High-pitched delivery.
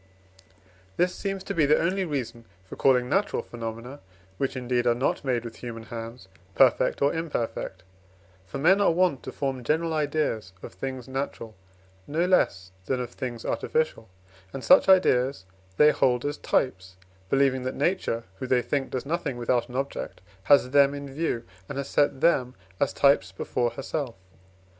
No: low, 135 Hz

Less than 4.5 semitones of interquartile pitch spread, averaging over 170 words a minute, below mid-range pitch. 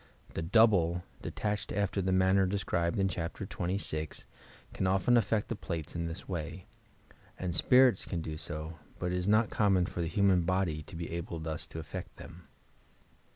Yes: average, 3.1 semitones; average, 180 wpm; very low, 90 Hz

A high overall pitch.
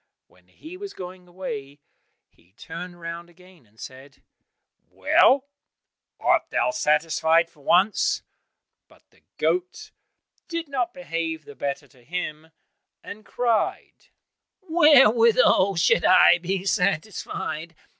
No: medium, 180 Hz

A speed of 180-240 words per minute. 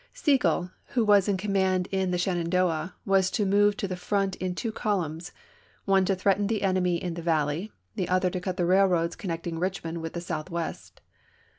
Yes: average, 185 wpm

